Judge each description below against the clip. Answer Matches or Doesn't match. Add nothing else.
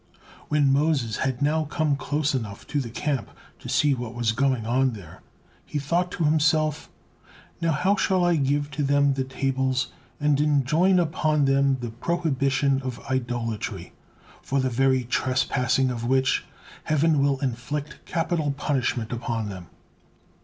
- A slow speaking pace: Doesn't match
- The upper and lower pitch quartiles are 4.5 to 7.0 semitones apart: Doesn't match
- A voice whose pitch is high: Doesn't match